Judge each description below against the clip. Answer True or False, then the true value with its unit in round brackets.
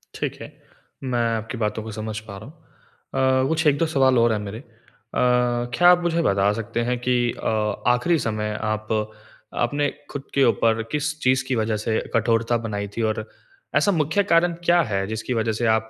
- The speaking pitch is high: False (120 Hz)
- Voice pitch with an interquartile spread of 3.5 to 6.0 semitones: True (4.0 semitones)